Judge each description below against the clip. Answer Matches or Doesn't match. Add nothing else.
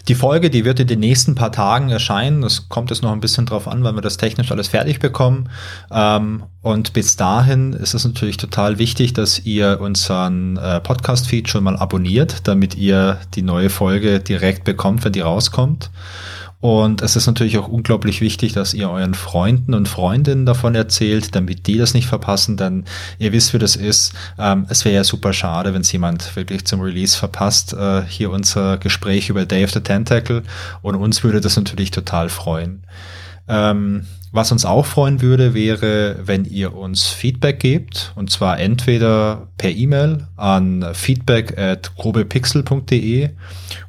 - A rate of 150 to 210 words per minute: Matches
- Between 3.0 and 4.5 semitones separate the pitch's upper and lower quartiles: Matches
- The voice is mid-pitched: Doesn't match